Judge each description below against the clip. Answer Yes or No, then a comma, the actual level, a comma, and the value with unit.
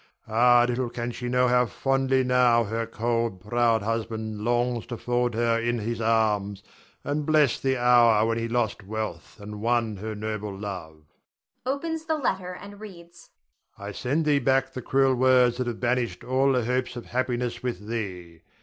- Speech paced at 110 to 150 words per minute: No, average, 175 wpm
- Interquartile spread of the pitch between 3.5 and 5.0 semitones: No, average, 2.7 semitones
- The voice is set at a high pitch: No, low, 120 Hz